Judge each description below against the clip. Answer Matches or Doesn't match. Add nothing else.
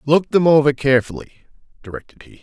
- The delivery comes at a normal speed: Matches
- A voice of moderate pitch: Matches